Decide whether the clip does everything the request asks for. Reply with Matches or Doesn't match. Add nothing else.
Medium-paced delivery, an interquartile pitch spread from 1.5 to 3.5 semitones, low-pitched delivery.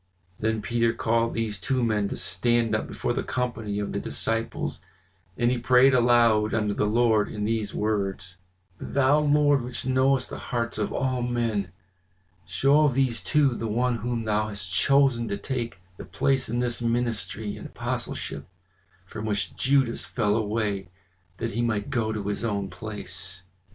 Matches